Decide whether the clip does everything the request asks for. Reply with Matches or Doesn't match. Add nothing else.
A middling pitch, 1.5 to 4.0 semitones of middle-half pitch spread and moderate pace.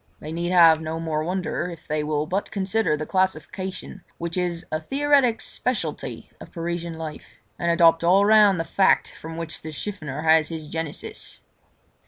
Matches